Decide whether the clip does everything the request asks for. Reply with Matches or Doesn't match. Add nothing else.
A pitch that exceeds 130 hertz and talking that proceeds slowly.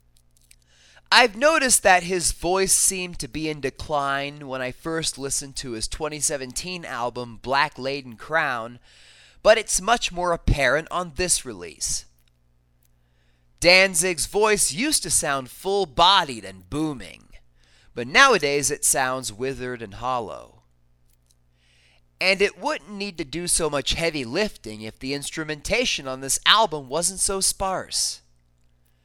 Matches